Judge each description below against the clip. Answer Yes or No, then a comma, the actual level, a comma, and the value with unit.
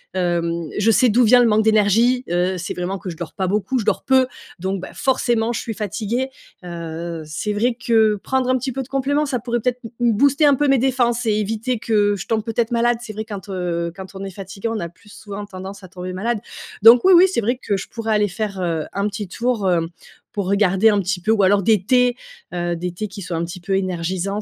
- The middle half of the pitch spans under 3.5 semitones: No, average, 4.2 semitones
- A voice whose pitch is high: Yes, high, 210 Hz